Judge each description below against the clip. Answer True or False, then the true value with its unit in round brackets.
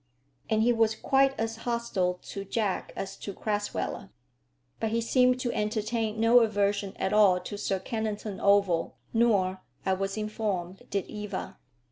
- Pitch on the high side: True (210 Hz)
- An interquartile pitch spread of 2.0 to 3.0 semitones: True (2.5 semitones)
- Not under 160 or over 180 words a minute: False (150 wpm)